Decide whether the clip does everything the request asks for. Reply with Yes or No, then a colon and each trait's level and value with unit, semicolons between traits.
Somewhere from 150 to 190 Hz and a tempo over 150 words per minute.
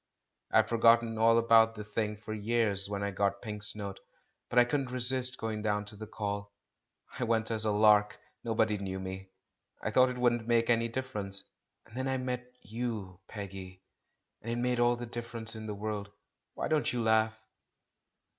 No: low, 110 Hz; average, 190 wpm